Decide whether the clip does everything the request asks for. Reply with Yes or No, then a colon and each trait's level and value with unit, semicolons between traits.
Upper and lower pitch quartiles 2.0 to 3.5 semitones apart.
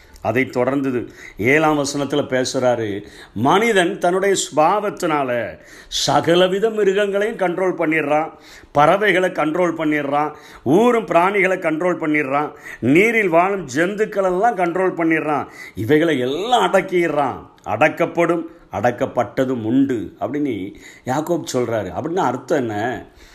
No: average, 4.5 semitones